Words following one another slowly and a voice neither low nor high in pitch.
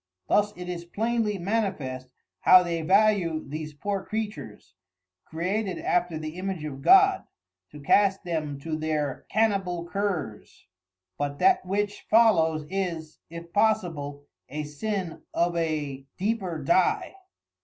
Yes: slow, 125 wpm; medium, 175 Hz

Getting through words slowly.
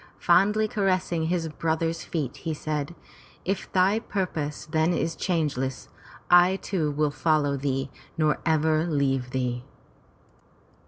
Yes: slow, 125 wpm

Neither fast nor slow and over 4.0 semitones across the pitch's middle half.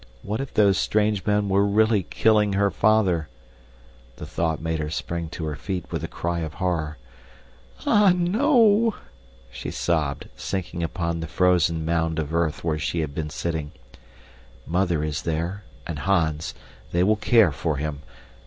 Yes: average, 160 wpm; average, 4.5 semitones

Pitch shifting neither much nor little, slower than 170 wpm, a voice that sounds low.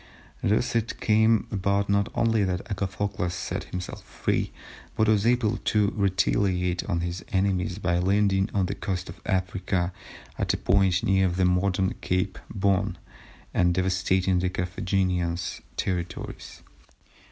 No: narrow, 1.9 semitones; slow, 135 wpm; very low, 95 Hz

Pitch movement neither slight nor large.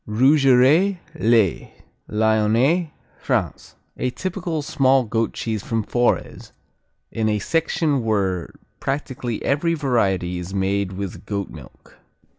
No: wide, 5.9 semitones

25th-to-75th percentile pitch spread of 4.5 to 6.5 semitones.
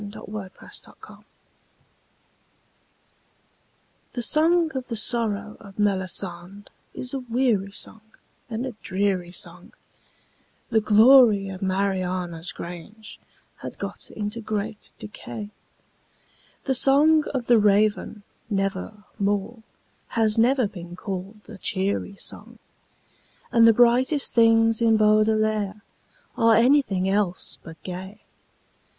No: average, 3.0 semitones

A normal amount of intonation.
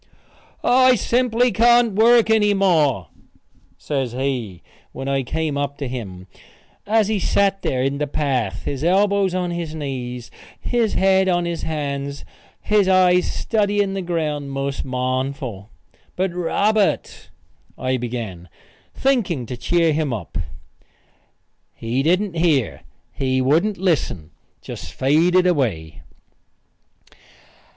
No: wide, 6.9 semitones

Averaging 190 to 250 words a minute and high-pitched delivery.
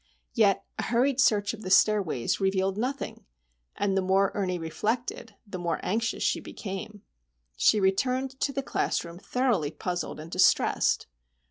No: average, 145 wpm; high, 200 Hz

